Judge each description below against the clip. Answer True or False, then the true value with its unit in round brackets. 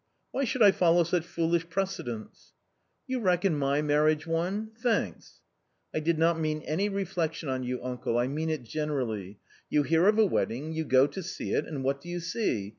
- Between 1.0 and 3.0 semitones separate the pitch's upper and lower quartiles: False (4.3 semitones)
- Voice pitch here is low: False (160 Hz)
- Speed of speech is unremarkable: False (210 wpm)